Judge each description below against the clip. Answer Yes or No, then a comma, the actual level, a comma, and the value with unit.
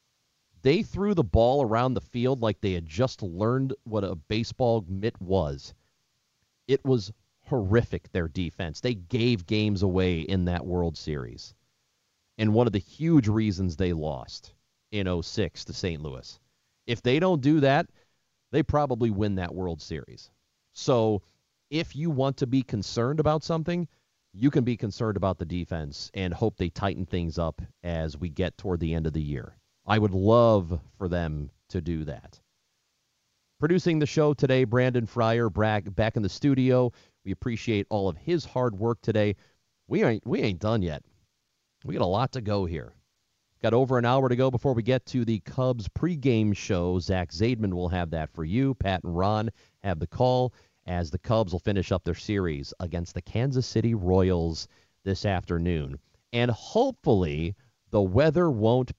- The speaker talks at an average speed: Yes, average, 175 wpm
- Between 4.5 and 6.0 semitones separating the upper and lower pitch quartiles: Yes, wide, 5.5 semitones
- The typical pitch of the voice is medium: No, low, 105 Hz